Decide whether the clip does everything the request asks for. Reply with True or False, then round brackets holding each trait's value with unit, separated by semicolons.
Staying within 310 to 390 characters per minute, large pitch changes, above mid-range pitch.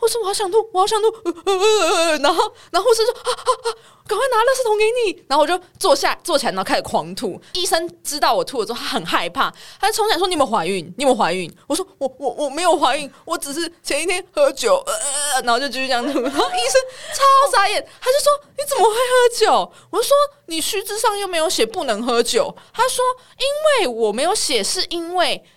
True (340 characters per minute; 7.3 semitones; 345 Hz)